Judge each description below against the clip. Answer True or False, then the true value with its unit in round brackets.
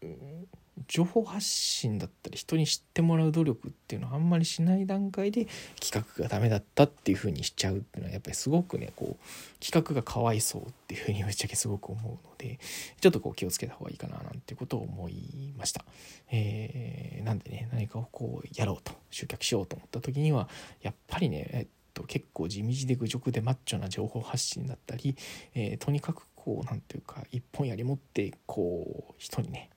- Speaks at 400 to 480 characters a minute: True (410 characters per minute)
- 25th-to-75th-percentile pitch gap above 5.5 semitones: False (5.1 semitones)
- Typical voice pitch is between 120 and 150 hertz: True (135 Hz)